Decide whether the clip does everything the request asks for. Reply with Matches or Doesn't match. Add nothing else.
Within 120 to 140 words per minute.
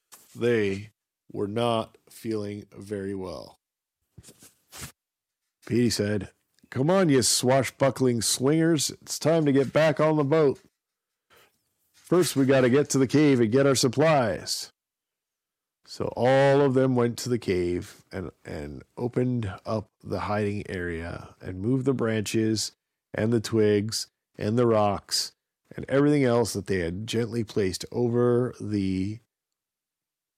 Matches